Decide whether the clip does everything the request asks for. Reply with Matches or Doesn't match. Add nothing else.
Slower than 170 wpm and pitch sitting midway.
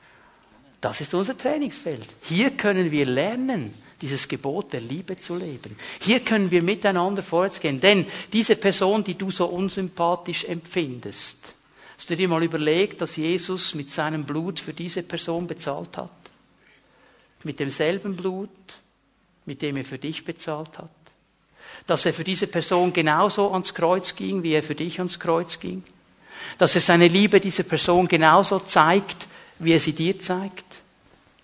Matches